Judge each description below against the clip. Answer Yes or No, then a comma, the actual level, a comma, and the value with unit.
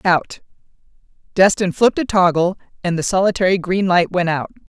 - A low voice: No, medium, 185 Hz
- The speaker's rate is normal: Yes, average, 150 wpm